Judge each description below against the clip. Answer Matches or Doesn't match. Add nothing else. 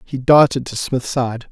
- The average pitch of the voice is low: Matches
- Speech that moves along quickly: Doesn't match